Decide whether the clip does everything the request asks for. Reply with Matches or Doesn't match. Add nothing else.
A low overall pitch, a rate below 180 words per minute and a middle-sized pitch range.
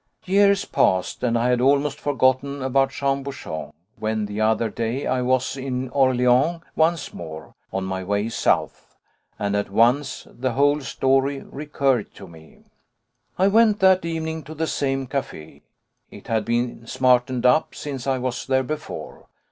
Matches